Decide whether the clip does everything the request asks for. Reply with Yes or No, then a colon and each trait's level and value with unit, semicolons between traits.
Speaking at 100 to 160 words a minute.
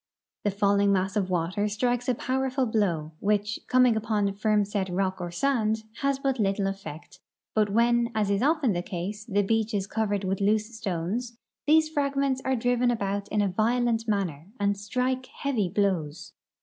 No: average, 175 wpm